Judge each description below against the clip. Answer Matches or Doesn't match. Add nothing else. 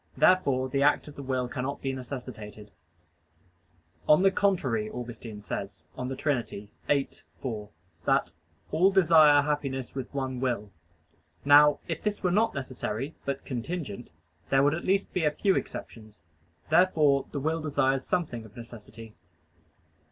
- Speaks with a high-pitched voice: Doesn't match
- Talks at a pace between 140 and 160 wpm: Matches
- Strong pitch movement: Doesn't match